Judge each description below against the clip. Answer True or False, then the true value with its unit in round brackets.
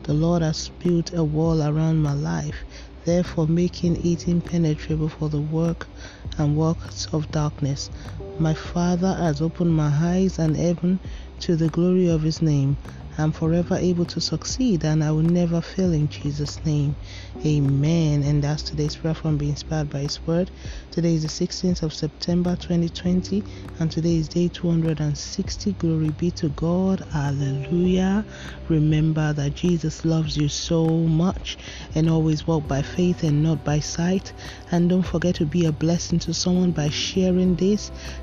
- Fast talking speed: False (160 wpm)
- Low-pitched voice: False (160 Hz)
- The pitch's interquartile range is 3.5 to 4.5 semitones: False (2.6 semitones)